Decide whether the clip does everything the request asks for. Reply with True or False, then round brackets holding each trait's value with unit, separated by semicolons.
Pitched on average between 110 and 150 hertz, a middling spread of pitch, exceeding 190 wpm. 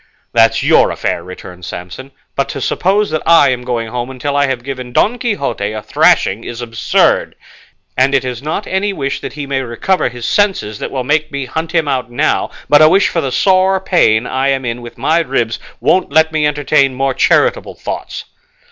True (135 Hz; 4.7 semitones; 200 wpm)